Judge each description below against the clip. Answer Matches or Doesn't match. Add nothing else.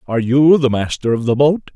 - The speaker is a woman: Doesn't match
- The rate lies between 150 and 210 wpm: Doesn't match